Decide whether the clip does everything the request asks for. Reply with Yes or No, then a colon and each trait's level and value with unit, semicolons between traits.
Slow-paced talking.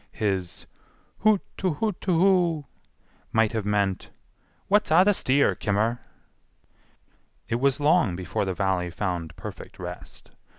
Yes: slow, 130 wpm